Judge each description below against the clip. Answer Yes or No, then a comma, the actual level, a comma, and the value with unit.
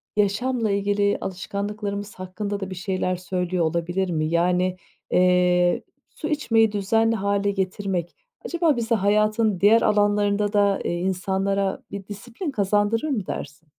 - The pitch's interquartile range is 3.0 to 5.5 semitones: No, narrow, 2.4 semitones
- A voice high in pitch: Yes, high, 200 Hz